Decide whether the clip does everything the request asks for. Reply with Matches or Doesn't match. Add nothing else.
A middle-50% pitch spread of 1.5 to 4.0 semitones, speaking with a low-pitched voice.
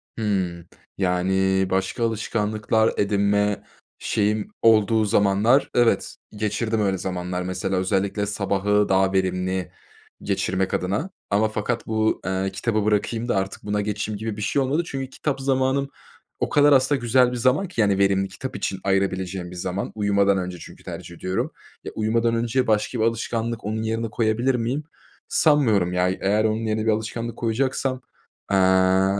Matches